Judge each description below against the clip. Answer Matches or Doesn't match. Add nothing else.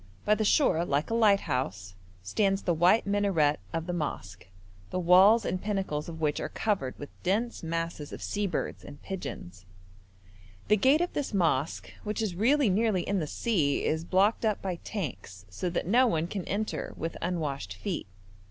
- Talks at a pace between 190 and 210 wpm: Doesn't match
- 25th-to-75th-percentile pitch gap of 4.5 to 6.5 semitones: Matches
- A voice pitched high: Doesn't match